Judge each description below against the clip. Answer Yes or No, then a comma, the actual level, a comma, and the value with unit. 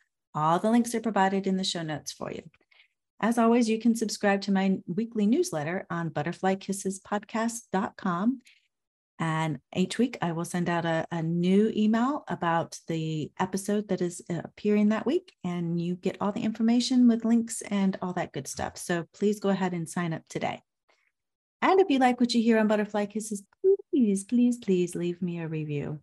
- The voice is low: No, high, 195 Hz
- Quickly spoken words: No, average, 180 wpm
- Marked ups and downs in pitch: No, average, 4.6 semitones